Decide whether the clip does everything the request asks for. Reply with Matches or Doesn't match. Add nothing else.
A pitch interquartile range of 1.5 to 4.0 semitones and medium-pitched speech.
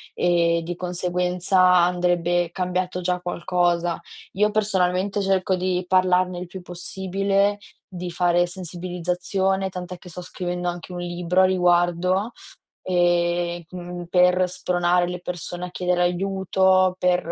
Doesn't match